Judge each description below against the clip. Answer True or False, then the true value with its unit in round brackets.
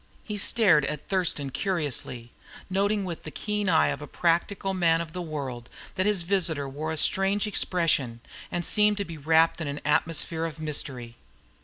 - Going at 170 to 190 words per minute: True (175 wpm)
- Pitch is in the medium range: True (165 Hz)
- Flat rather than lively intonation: False (4.5 semitones)